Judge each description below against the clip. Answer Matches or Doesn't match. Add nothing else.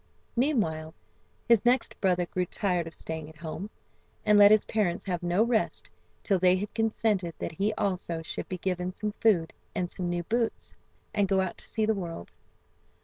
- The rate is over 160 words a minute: Matches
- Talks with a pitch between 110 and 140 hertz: Doesn't match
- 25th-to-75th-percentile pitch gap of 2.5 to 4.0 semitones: Matches